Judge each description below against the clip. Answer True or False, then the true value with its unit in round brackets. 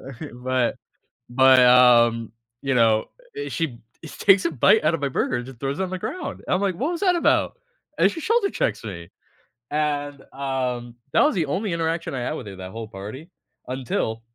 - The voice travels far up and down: True (5.9 semitones)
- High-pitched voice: False (135 Hz)